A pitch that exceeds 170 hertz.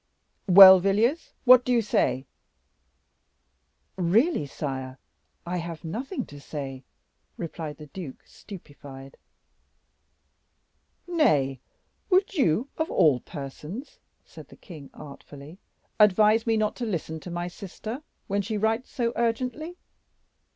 Yes: high, 190 Hz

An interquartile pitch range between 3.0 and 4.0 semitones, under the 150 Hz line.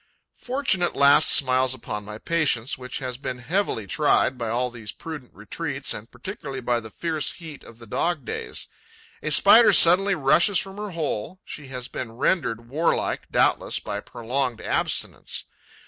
No: wide, 5.6 semitones; low, 135 Hz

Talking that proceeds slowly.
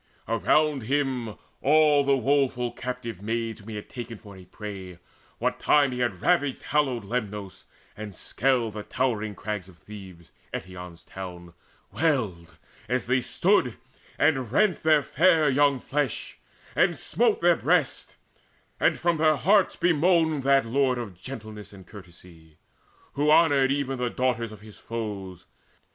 No: average, 150 wpm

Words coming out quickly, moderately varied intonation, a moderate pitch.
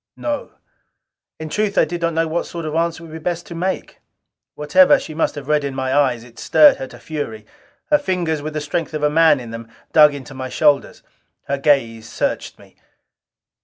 Yes: fast, 210 wpm; average, 3.6 semitones; medium, 155 Hz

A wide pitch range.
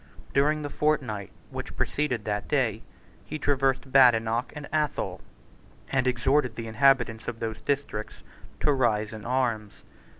No: average, 4.0 semitones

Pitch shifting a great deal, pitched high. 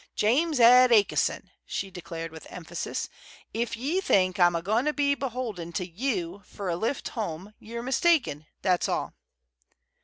Yes: wide, 6.4 semitones; high, 215 Hz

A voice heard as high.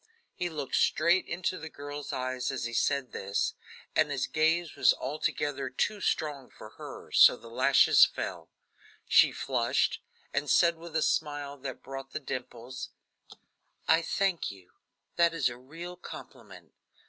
No: medium, 145 Hz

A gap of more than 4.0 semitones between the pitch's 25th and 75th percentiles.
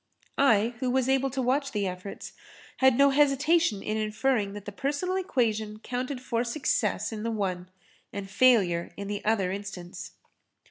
Yes: average, 4.7 semitones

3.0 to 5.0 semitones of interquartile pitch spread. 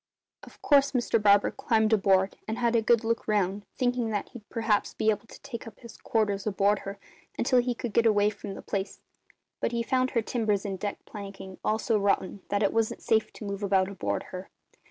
No: narrow, 2.5 semitones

